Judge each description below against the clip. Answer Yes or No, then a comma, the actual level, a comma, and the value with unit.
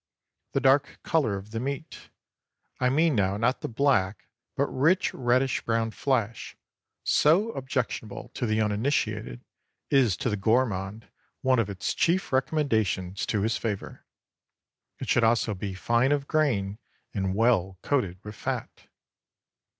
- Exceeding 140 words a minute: No, slow, 135 wpm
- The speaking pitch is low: Yes, low, 115 Hz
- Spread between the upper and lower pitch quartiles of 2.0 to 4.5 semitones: No, average, 4.9 semitones